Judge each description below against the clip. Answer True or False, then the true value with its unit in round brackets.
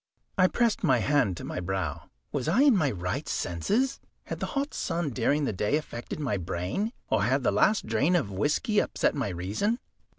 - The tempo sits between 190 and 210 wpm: True (195 wpm)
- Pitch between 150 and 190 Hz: False (140 Hz)